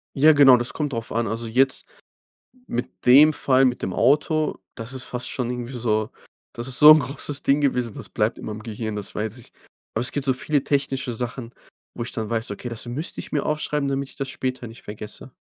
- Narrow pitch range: No, average, 3.1 semitones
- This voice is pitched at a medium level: No, low, 125 Hz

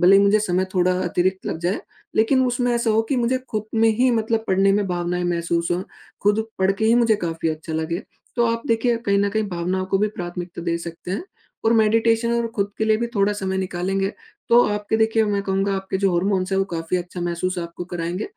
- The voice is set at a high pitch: Yes, high, 195 Hz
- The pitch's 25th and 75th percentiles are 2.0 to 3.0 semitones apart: No, average, 3.7 semitones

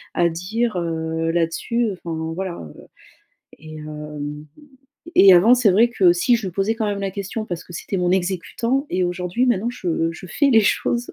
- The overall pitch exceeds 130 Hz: Yes, medium, 185 Hz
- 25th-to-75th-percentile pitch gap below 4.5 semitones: No, average, 5.1 semitones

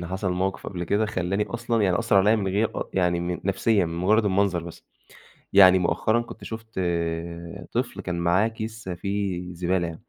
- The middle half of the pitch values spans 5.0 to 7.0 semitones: No, average, 3.4 semitones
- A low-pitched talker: Yes, very low, 95 Hz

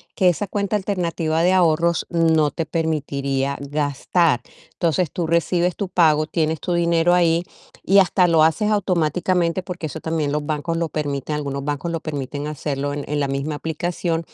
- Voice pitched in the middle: Yes, medium, 165 Hz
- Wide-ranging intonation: No, average, 2.9 semitones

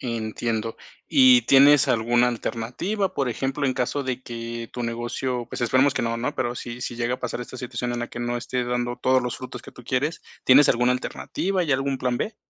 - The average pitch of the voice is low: Yes, low, 125 Hz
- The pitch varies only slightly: Yes, narrow, 2.0 semitones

